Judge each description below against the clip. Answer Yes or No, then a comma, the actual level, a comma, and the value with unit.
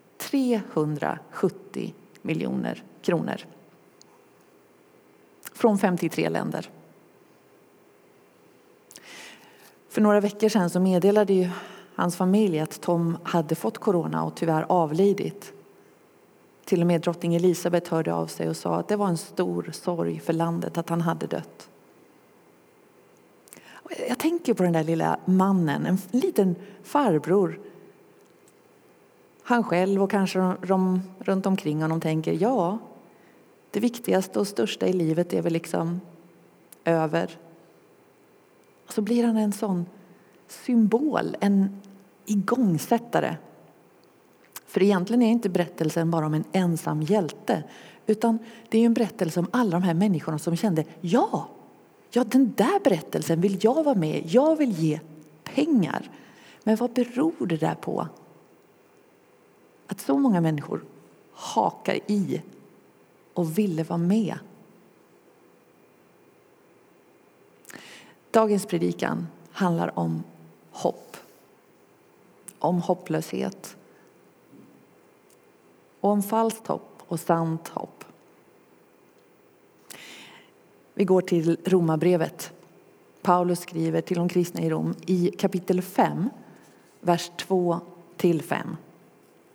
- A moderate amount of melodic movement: Yes, average, 3.9 semitones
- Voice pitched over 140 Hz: Yes, medium, 185 Hz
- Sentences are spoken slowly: Yes, slow, 110 wpm